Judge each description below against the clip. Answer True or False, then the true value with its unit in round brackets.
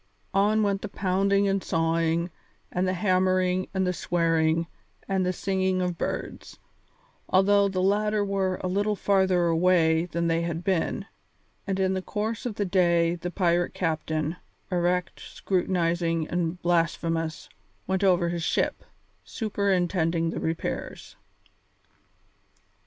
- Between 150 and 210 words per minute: False (135 wpm)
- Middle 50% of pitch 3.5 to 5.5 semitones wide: False (2.4 semitones)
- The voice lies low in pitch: False (180 Hz)